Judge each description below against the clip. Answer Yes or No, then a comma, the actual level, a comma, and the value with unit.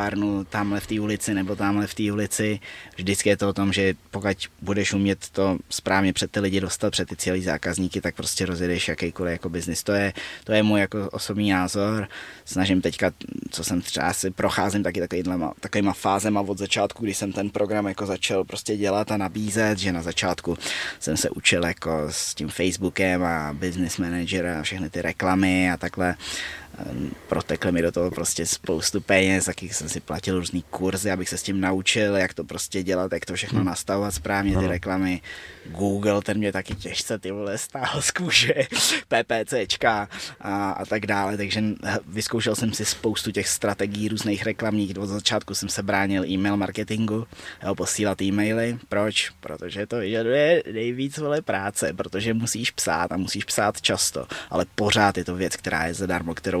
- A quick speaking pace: Yes, fast, 180 wpm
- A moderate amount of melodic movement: No, narrow, 2.3 semitones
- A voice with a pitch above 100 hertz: No, very low, 95 Hz